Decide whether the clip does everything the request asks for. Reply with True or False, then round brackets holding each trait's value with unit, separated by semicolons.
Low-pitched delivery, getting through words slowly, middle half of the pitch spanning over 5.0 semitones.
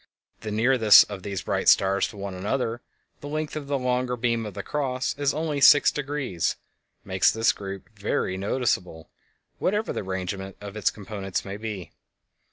False (110 Hz; 155 wpm; 5.4 semitones)